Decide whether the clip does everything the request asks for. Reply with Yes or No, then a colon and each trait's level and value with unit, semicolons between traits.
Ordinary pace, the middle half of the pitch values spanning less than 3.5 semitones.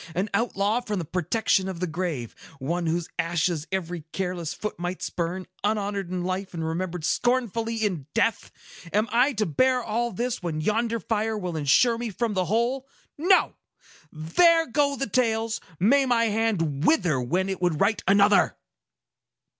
No: average, 160 wpm; average, 4.8 semitones